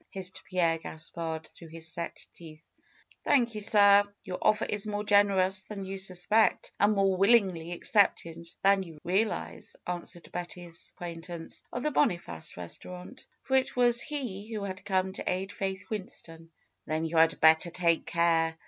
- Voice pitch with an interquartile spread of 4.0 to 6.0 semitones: No, average, 3.4 semitones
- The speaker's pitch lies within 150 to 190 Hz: Yes, medium, 185 Hz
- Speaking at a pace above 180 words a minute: No, average, 160 wpm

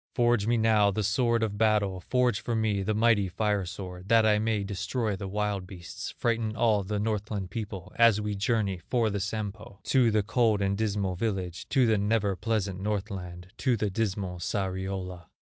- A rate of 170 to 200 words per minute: Yes, average, 180 wpm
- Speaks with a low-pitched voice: Yes, low, 105 Hz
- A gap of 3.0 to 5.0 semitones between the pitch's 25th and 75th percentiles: No, narrow, 2.5 semitones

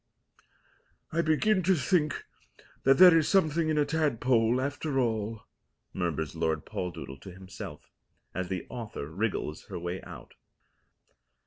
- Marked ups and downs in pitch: Yes, wide, 9.0 semitones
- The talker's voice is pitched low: Yes, low, 125 Hz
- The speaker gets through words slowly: Yes, slow, 130 wpm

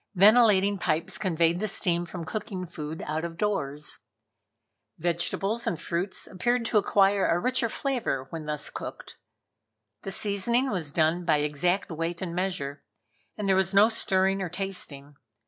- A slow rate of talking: No, average, 150 wpm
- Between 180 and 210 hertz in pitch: Yes, medium, 185 Hz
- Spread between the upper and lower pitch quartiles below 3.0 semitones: No, average, 3.8 semitones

